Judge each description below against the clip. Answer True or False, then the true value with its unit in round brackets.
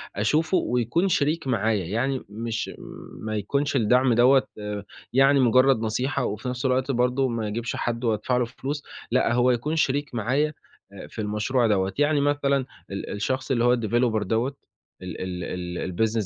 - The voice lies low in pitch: True (125 Hz)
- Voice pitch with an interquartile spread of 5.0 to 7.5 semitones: False (3.7 semitones)